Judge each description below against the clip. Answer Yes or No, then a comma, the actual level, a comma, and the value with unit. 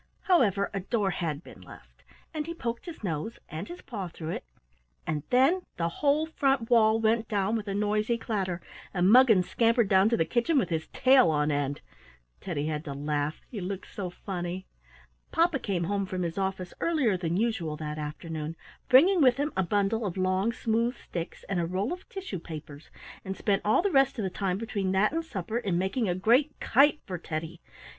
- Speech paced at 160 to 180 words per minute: No, average, 200 wpm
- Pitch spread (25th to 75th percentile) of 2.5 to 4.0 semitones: No, wide, 5.4 semitones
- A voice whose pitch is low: No, high, 200 Hz